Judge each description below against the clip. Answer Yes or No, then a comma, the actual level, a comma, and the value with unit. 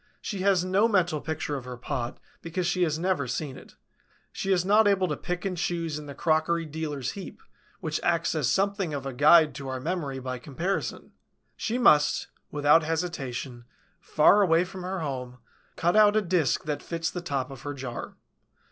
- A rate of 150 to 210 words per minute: Yes, average, 190 wpm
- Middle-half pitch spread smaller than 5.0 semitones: Yes, average, 4.4 semitones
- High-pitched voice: No, medium, 160 Hz